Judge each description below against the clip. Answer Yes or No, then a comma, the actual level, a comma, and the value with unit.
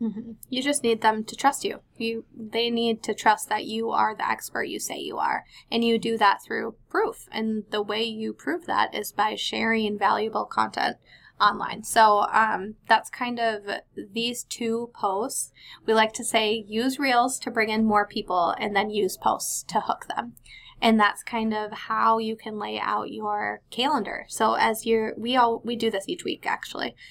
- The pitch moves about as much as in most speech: No, narrow, 1.5 semitones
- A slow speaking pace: No, average, 195 wpm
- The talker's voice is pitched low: No, high, 225 Hz